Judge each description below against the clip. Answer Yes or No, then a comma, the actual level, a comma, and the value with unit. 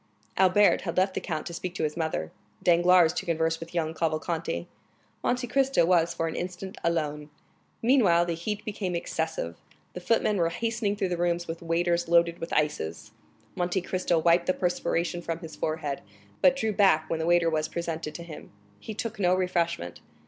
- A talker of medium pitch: Yes, medium, 170 Hz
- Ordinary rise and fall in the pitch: No, narrow, 2.1 semitones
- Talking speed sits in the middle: Yes, average, 185 wpm